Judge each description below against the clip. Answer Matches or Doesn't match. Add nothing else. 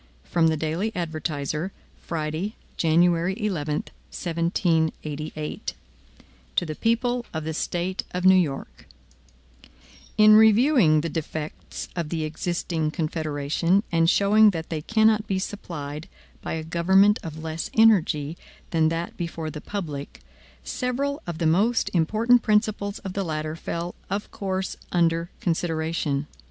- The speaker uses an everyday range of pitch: Matches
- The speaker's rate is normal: Doesn't match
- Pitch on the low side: Doesn't match